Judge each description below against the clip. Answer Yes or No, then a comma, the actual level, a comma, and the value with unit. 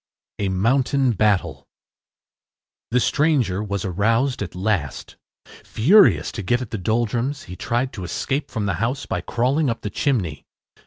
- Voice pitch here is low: Yes, low, 115 Hz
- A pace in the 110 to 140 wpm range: No, average, 150 wpm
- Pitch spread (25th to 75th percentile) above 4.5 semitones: Yes, average, 5.2 semitones